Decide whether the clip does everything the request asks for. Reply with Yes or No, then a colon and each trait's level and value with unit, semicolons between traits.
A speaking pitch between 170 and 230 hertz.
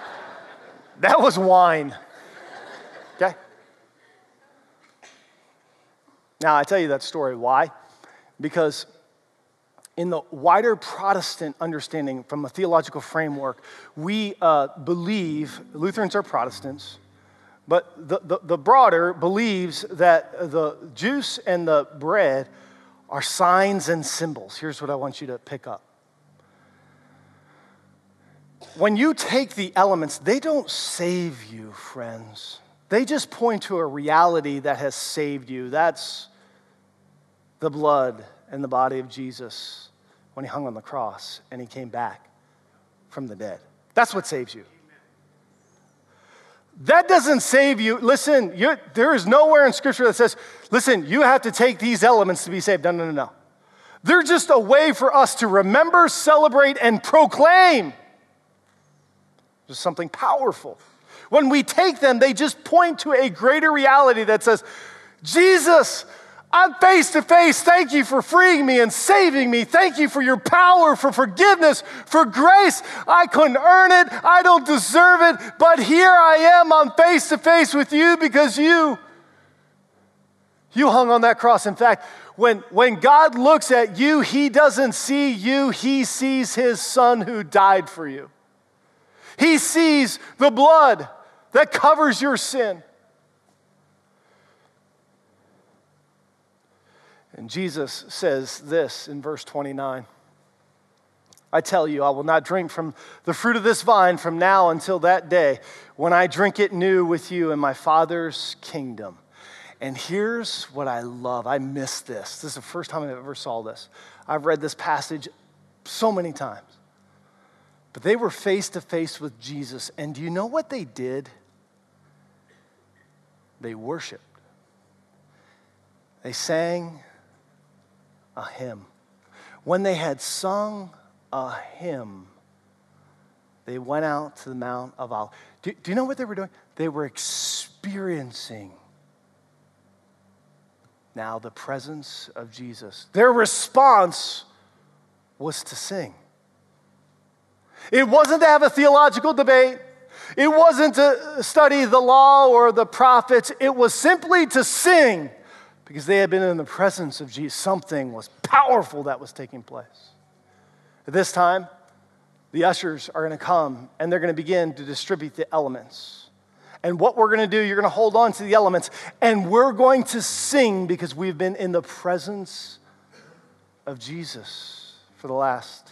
Yes: high, 190 Hz